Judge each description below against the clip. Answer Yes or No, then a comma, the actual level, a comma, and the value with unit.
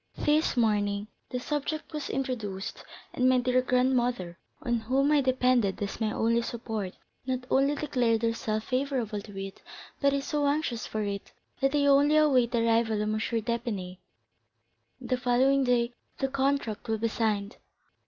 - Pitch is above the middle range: Yes, high, 245 Hz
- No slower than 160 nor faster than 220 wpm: Yes, average, 165 wpm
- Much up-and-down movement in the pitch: No, average, 3.8 semitones